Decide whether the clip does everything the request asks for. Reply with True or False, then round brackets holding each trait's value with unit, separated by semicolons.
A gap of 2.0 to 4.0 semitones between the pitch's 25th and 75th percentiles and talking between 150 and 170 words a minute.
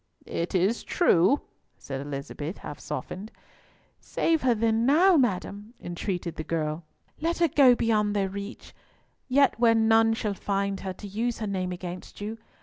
False (4.6 semitones; 155 wpm)